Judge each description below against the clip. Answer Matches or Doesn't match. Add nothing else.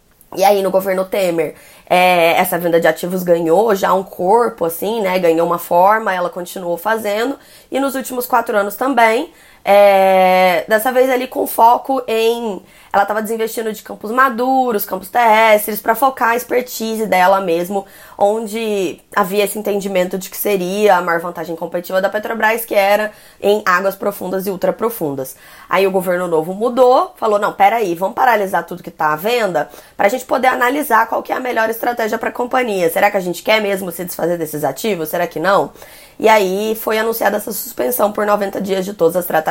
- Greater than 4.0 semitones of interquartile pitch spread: Doesn't match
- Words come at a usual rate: Doesn't match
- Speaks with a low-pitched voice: Doesn't match